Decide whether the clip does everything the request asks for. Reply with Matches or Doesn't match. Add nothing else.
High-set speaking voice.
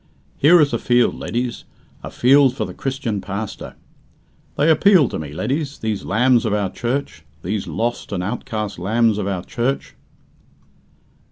Doesn't match